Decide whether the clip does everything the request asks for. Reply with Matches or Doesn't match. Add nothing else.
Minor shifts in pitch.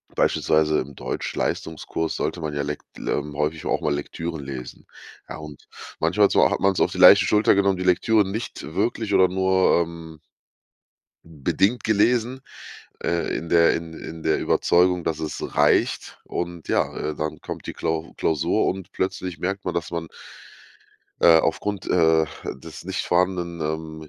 Doesn't match